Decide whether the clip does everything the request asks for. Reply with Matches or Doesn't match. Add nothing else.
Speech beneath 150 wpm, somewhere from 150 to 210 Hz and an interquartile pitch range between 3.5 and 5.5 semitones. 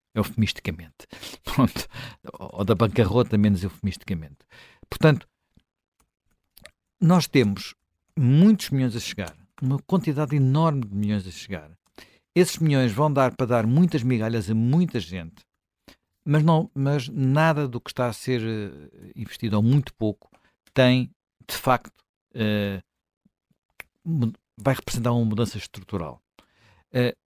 Doesn't match